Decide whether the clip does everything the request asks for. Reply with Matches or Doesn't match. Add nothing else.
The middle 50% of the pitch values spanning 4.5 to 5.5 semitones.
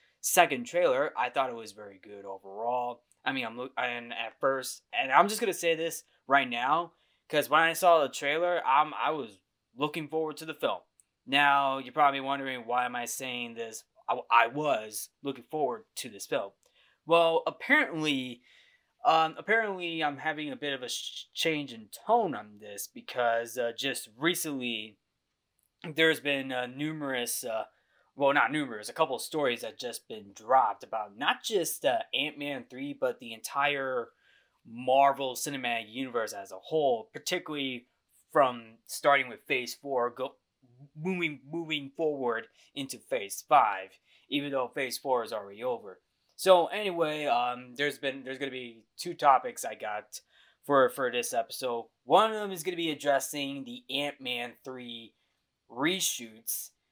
Matches